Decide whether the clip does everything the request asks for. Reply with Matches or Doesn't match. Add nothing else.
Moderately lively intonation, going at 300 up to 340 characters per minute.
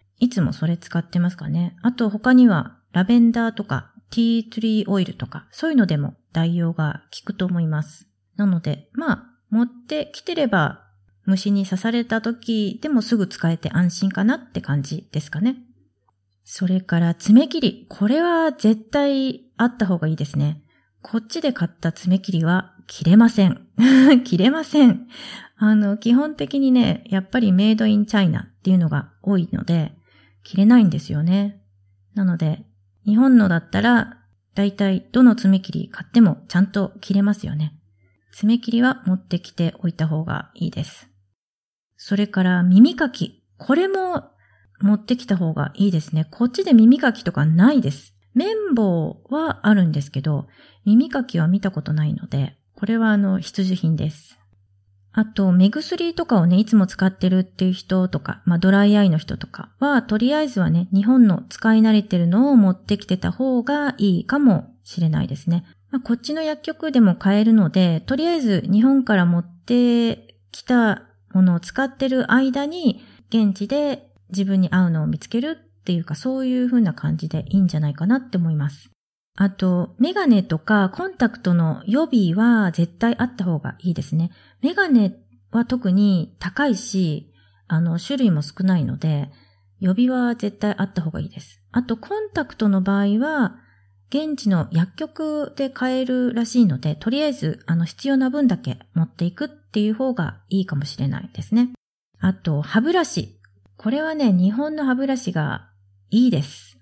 Doesn't match